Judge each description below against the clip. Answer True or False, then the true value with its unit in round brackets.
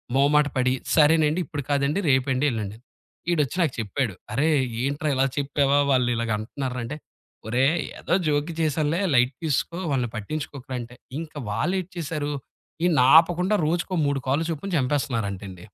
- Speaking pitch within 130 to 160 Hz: True (140 Hz)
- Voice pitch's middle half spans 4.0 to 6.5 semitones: False (3.6 semitones)